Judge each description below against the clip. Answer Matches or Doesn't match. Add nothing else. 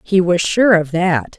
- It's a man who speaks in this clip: Doesn't match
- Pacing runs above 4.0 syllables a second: Doesn't match